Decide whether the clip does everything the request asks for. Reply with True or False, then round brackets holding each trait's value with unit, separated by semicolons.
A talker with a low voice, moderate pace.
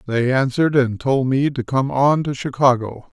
True (130 Hz; 190 wpm)